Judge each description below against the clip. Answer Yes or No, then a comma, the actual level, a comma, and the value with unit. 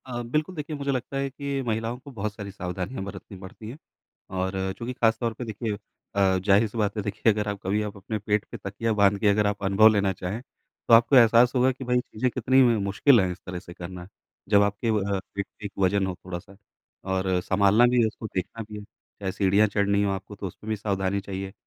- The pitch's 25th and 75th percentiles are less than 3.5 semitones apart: Yes, average, 3.1 semitones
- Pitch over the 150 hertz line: No, low, 105 Hz